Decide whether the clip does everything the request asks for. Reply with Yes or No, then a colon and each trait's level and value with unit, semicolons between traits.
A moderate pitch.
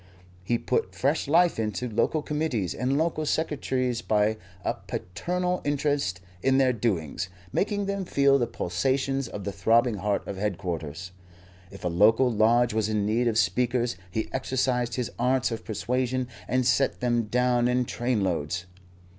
No: low, 120 Hz